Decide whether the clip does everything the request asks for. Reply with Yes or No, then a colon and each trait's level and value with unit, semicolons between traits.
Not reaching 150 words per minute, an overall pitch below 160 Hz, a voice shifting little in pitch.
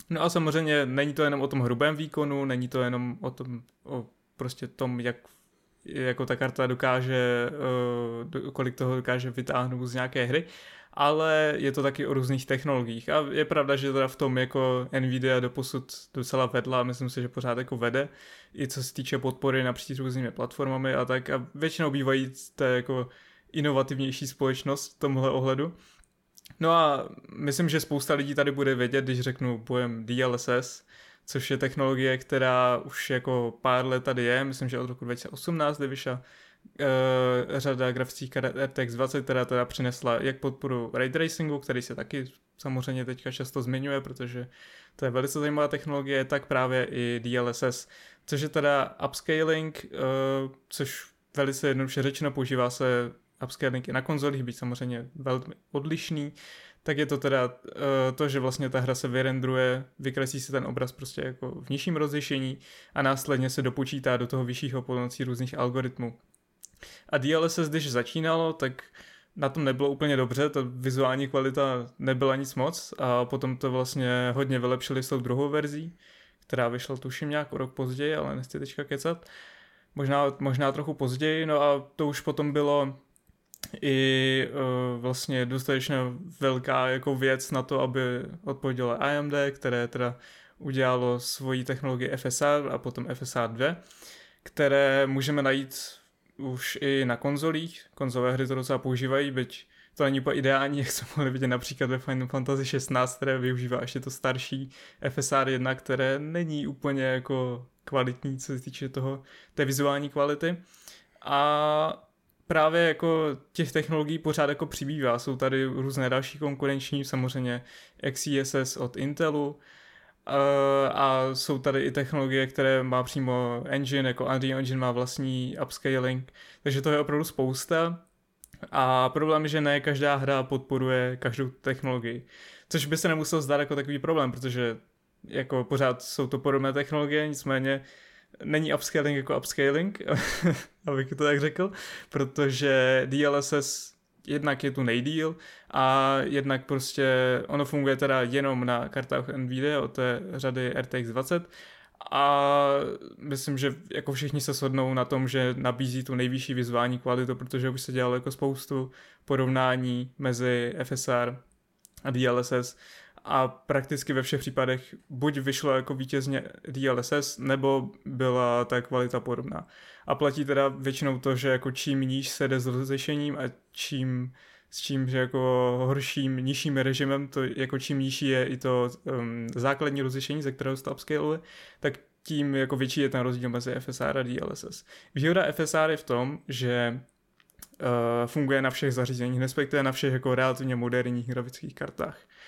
No: average, 155 wpm; low, 135 Hz; narrow, 1.8 semitones